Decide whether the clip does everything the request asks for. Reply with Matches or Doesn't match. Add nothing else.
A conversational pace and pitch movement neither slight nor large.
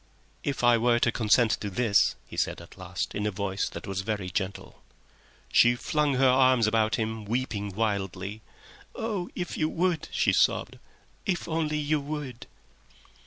Doesn't match